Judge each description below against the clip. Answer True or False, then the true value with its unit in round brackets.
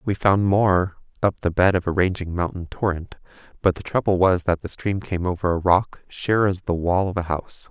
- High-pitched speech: False (90 Hz)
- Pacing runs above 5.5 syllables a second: False (5.1 syllables/s)